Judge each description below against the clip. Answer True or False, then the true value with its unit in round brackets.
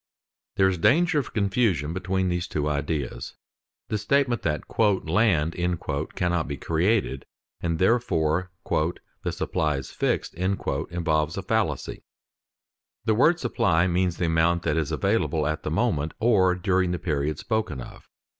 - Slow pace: False (145 wpm)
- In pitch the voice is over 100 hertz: False (90 Hz)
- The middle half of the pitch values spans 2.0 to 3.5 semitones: False (4.3 semitones)